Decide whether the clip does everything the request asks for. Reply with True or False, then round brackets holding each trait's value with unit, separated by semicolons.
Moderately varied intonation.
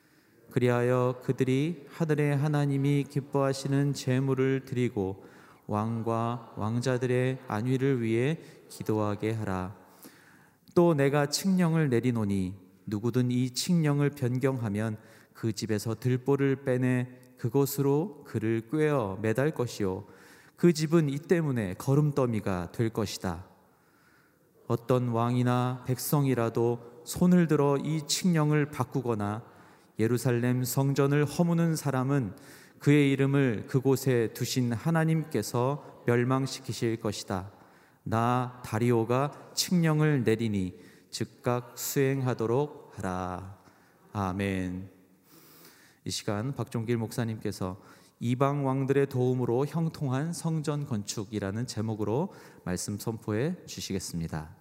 True (4.4 semitones)